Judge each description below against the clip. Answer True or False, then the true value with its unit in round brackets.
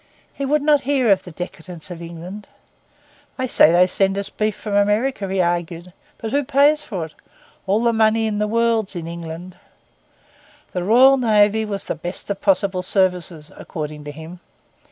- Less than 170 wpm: False (175 wpm)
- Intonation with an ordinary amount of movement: True (4.4 semitones)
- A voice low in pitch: False (200 Hz)